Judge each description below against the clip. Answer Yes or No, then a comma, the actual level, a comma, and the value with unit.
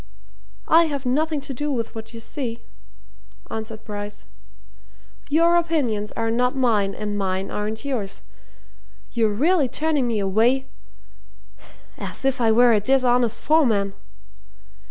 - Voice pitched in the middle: No, high, 240 Hz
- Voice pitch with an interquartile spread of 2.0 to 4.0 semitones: No, average, 4.6 semitones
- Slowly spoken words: Yes, slow, 130 wpm